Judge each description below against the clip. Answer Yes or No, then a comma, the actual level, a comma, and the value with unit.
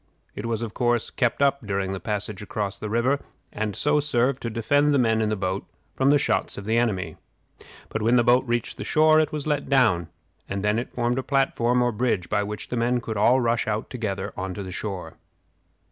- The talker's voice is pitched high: No, low, 115 Hz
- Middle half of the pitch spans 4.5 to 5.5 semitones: No, average, 3.6 semitones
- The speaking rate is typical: No, fast, 220 wpm